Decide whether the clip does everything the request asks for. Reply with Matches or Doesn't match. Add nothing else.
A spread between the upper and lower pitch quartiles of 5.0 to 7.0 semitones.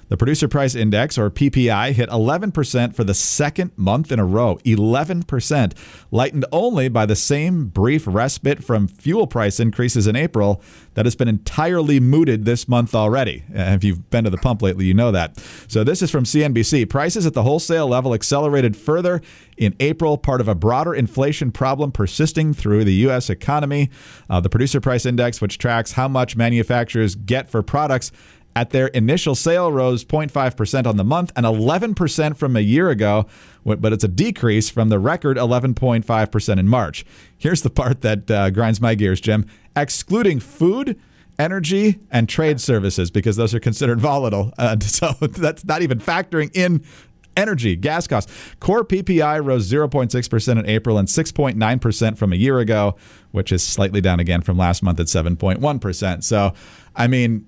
Matches